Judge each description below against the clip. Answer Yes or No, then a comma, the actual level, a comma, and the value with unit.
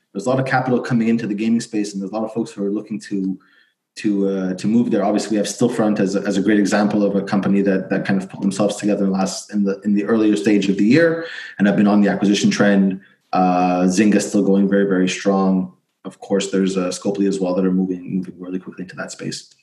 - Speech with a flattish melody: Yes, narrow, 1.5 semitones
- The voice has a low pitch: Yes, low, 100 Hz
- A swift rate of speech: Yes, fast, 265 wpm